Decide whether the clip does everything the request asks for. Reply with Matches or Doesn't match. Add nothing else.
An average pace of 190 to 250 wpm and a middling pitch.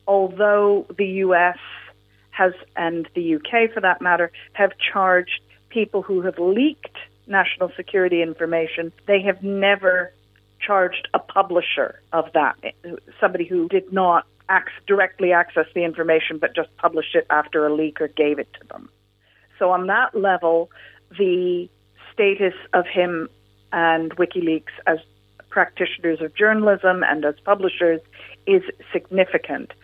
Doesn't match